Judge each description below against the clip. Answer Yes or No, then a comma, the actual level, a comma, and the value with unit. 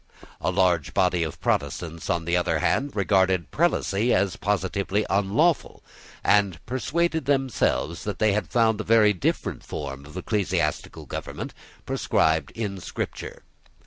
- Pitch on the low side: Yes, low, 100 Hz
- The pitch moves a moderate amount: Yes, average, 4.1 semitones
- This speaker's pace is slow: Yes, slow, 130 wpm